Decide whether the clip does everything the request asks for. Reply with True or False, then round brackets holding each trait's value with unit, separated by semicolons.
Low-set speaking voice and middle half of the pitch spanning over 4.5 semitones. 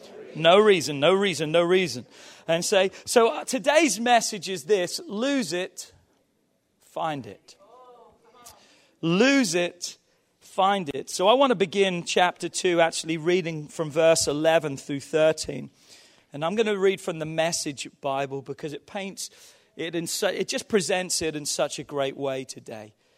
False (175 Hz; 5.2 semitones)